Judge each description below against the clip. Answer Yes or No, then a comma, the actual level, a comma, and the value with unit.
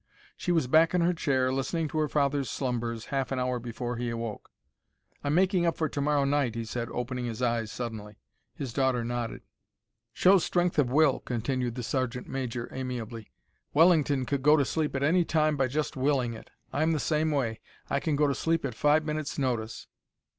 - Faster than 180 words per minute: Yes, average, 195 wpm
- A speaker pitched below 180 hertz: Yes, low, 135 Hz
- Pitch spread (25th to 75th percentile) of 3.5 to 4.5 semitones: Yes, average, 4.0 semitones